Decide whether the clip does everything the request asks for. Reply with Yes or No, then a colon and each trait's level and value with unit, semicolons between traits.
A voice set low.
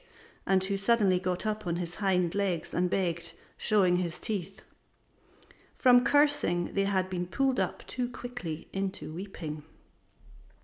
No: high, 190 Hz